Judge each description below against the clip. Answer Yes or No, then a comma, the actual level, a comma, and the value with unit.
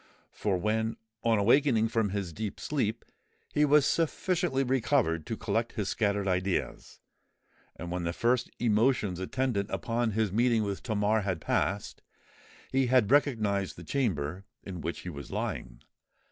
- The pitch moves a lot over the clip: No, average, 4.2 semitones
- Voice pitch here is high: No, low, 110 Hz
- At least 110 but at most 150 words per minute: Yes, average, 140 wpm